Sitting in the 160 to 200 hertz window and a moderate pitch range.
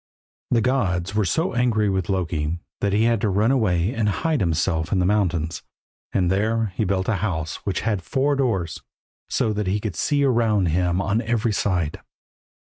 No: low, 100 Hz; average, 4.0 semitones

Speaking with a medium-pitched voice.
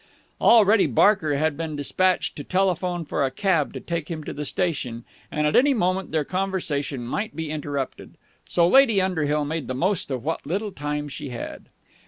Yes: medium, 160 Hz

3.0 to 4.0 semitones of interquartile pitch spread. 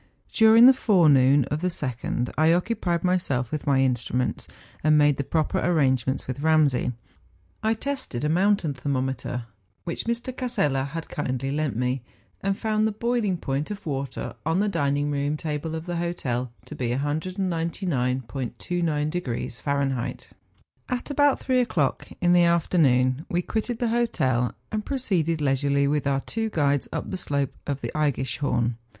No: wide, 5.4 semitones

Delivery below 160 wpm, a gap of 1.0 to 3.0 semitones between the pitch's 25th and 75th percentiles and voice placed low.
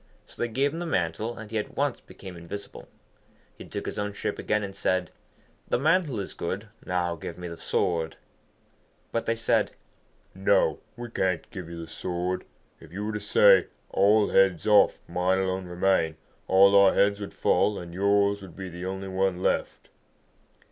No: average, 180 wpm; average, 2.7 semitones; very low, 95 Hz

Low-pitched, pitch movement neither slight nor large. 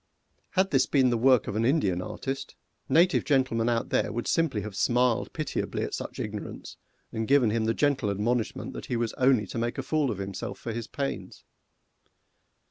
Yes: low, 120 Hz; average, 3.5 semitones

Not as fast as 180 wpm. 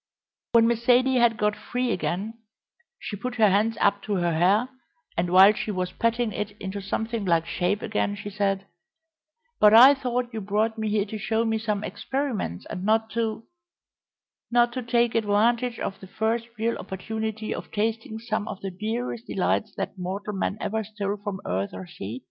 No: average, 185 wpm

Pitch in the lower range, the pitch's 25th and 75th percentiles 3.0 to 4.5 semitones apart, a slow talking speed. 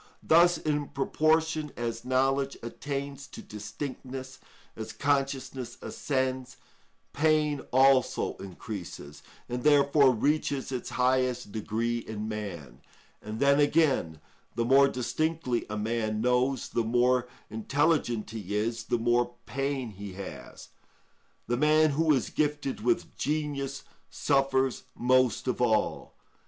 Yes: low, 130 Hz; average, 3.4 semitones; slow, 120 wpm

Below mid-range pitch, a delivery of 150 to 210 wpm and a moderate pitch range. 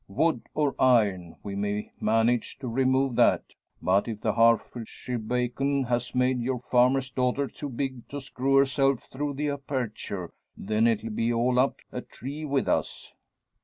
Yes: low, 125 Hz; average, 160 wpm; average, 3.0 semitones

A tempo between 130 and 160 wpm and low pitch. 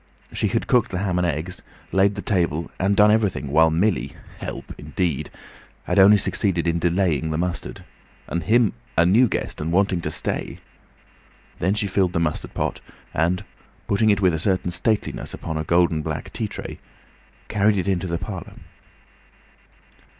No: average, 170 wpm; very low, 90 Hz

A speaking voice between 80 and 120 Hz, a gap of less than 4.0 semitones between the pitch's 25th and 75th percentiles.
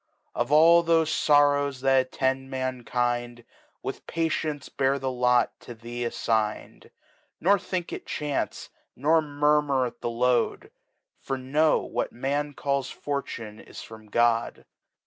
No: low, 135 Hz; average, 3.4 semitones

